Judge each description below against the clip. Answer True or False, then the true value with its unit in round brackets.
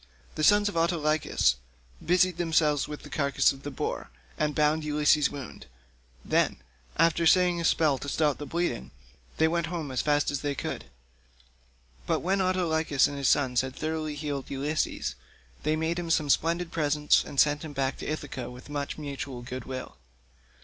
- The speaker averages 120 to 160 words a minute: False (175 wpm)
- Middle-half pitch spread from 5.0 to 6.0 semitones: False (2.7 semitones)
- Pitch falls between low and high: True (150 Hz)